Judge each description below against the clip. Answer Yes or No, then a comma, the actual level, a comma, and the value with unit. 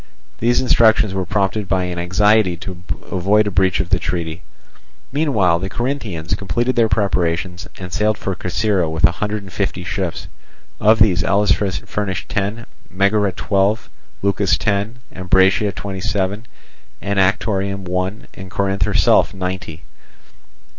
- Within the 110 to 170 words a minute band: Yes, average, 140 wpm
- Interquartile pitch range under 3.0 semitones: Yes, narrow, 2.4 semitones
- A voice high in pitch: No, very low, 95 Hz